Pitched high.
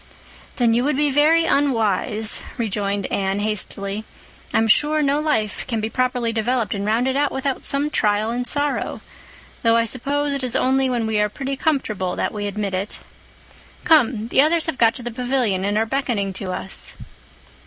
Yes: high, 235 Hz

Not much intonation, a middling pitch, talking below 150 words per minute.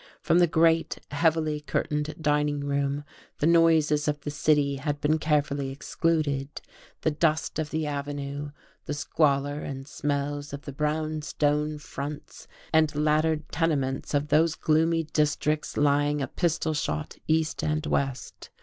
Yes: narrow, 1.5 semitones; medium, 150 Hz; average, 140 wpm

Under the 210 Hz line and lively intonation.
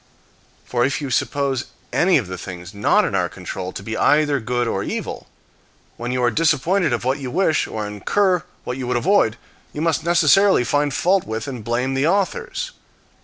Yes: low, 135 Hz; wide, 5.8 semitones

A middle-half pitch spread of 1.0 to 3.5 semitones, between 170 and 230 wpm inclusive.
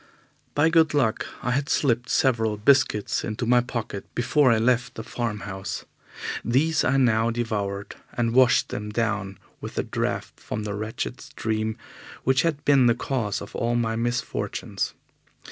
No: average, 3.1 semitones; average, 160 wpm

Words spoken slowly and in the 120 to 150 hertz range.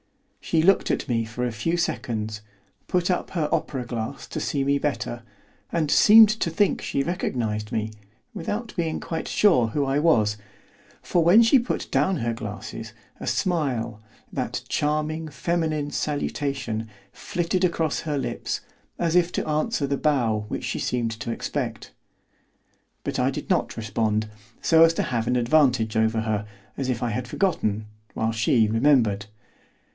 No: average, 160 wpm; medium, 140 Hz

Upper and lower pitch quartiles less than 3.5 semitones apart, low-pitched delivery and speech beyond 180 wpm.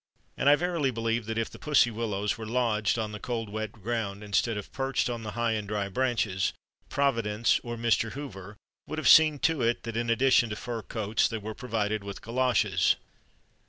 Yes: average, 2.8 semitones; low, 115 Hz; average, 195 wpm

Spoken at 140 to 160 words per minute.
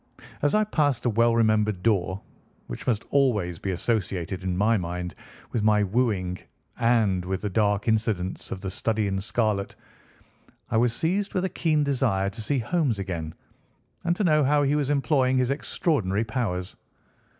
No: average, 170 wpm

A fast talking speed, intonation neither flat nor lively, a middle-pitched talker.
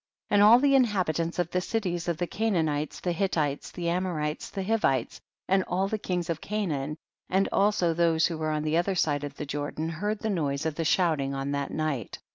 Yes: fast, 215 wpm; average, 4.1 semitones; medium, 170 Hz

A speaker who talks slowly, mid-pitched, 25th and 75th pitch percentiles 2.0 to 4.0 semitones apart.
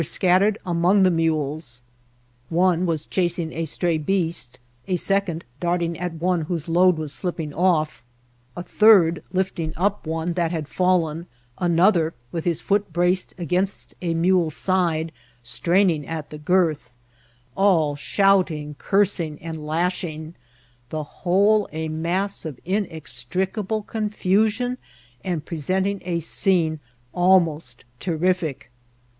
Yes: slow, 125 wpm; medium, 175 Hz; average, 2.9 semitones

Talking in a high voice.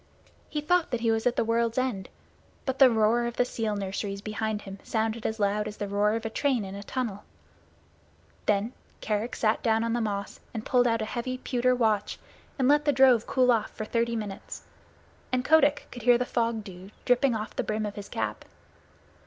Yes: high, 225 Hz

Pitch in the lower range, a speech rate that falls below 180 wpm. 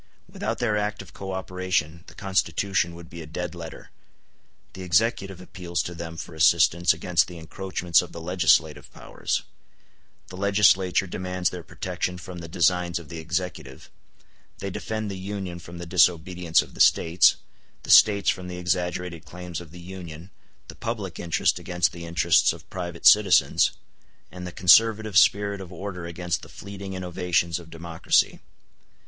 Yes: very low, 90 Hz; average, 160 wpm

